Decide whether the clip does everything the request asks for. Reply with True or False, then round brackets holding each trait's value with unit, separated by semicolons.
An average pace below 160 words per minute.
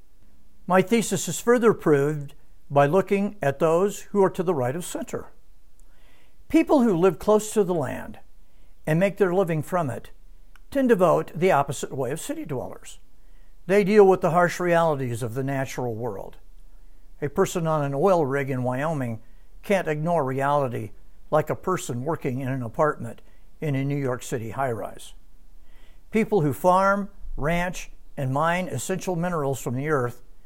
False (165 wpm)